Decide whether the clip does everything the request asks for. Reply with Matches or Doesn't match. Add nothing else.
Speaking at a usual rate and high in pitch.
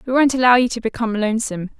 Doesn't match